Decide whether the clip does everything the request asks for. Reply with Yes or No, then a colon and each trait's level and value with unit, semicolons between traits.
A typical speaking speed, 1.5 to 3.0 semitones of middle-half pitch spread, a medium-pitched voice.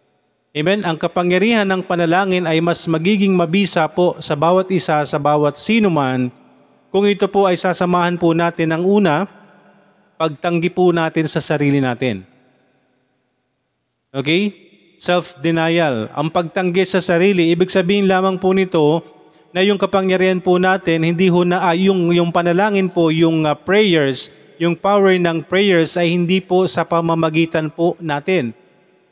Yes: average, 145 wpm; average, 2.7 semitones; medium, 175 Hz